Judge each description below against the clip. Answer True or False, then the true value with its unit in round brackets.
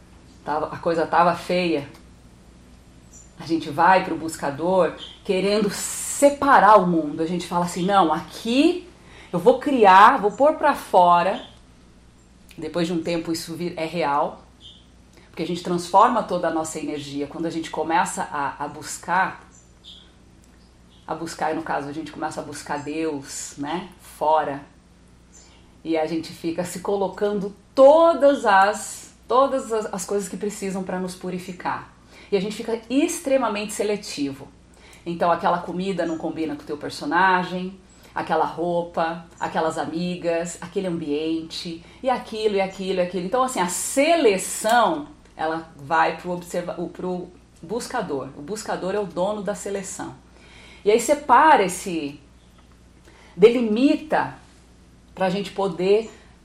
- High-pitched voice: False (175 Hz)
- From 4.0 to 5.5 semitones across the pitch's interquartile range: True (4.5 semitones)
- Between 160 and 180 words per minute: False (140 wpm)